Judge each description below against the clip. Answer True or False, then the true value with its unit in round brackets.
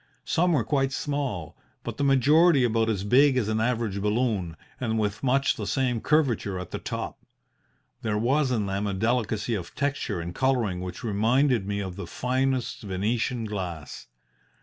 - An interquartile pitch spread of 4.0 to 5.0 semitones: True (4.6 semitones)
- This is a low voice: True (115 Hz)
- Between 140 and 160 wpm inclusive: False (170 wpm)